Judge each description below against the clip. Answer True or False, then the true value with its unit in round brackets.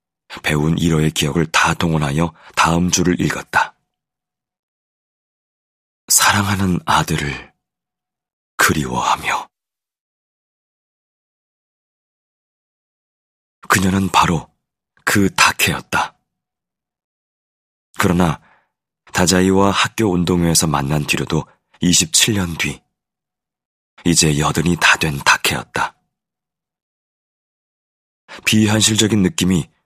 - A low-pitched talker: True (85 Hz)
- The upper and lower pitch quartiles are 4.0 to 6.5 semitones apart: False (3.3 semitones)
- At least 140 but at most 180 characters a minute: True (165 characters per minute)